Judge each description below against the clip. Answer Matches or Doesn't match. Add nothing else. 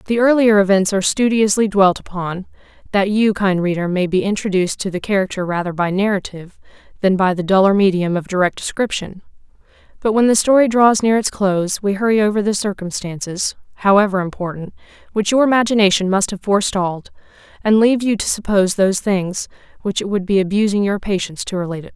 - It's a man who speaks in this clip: Doesn't match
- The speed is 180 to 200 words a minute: Matches